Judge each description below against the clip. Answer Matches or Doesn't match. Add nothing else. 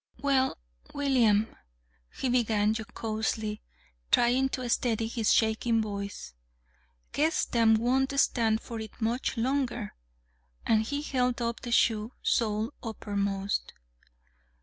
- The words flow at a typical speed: Doesn't match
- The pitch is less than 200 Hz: Doesn't match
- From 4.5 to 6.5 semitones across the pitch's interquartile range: Doesn't match